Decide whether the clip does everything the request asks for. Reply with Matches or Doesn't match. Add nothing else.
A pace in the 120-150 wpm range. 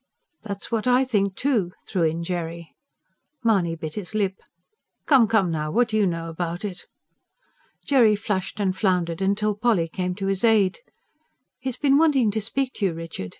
Doesn't match